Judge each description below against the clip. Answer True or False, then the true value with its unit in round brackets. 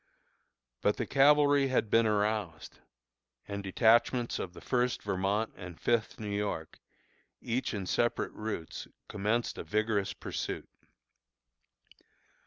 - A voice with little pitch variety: False (3.0 semitones)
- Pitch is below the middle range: True (110 Hz)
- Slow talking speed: True (115 wpm)